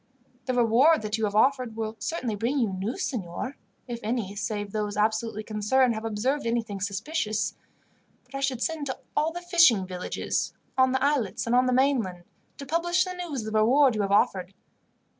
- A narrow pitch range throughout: No, average, 4.4 semitones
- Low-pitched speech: No, high, 230 Hz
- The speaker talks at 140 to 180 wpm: No, average, 190 wpm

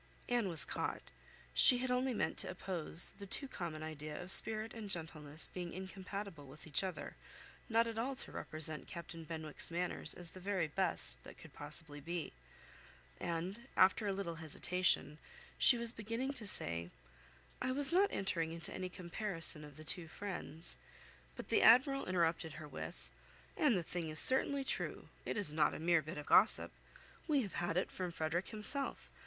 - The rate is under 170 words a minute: No, average, 175 wpm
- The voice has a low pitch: No, medium, 180 Hz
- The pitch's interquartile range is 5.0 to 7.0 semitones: Yes, wide, 5.4 semitones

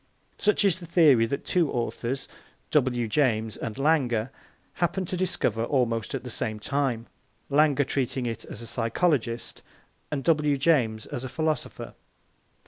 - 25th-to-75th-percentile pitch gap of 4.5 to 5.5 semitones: Yes, average, 4.8 semitones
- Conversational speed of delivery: Yes, average, 145 wpm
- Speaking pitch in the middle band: No, low, 130 Hz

